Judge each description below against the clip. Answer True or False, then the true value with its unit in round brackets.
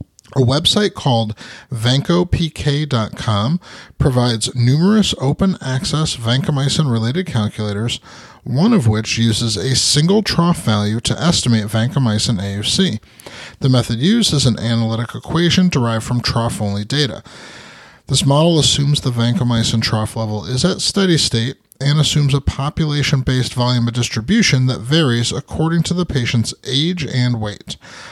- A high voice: False (130 Hz)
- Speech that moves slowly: True (130 wpm)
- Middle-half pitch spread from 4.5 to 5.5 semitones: True (4.9 semitones)